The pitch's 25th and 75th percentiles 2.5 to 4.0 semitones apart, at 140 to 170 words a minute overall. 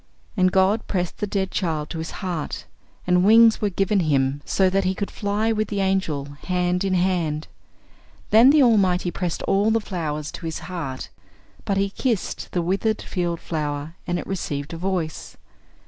No: average, 3.4 semitones; average, 180 wpm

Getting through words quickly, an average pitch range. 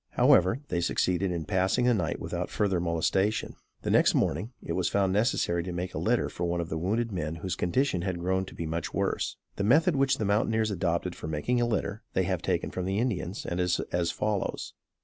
Yes: fast, 220 wpm; average, 3.6 semitones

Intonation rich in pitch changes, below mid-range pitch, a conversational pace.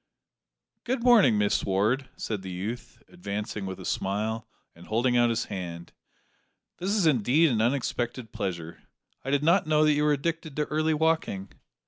Yes: wide, 7.1 semitones; low, 120 Hz; average, 165 wpm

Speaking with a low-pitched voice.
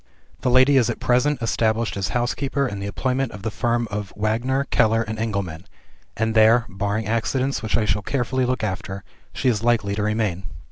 Yes: low, 110 Hz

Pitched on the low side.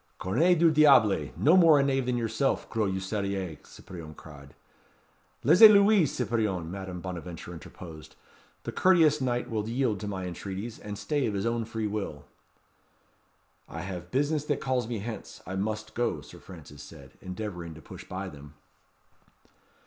Yes: low, 105 Hz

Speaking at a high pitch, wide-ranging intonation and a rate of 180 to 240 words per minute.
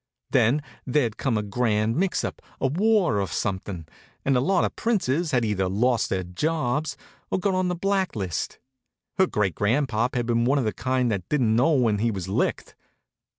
No: low, 125 Hz; wide, 6.3 semitones; average, 190 wpm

